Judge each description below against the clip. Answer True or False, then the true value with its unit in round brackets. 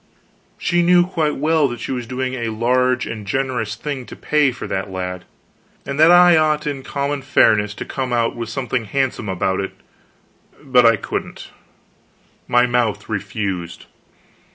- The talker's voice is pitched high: False (125 Hz)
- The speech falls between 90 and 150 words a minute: False (160 wpm)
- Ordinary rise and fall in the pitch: True (4.5 semitones)